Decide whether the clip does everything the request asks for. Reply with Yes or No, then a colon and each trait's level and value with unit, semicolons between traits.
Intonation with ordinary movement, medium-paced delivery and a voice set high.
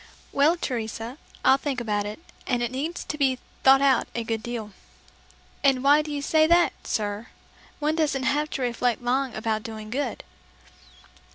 Yes: average, 4.2 semitones; average, 170 wpm; very high, 260 Hz